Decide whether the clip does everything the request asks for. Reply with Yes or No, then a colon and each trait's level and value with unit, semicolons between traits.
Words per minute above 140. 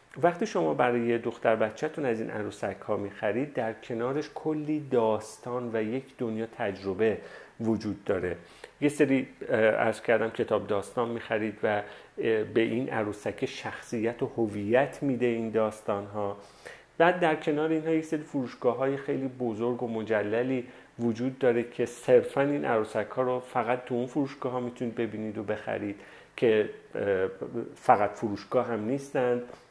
Yes: fast, 155 wpm